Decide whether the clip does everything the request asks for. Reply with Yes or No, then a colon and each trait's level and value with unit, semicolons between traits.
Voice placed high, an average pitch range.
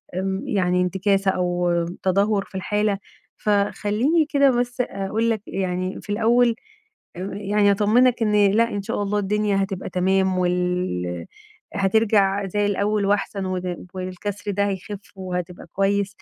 No: high, 200 Hz; narrow, 2.0 semitones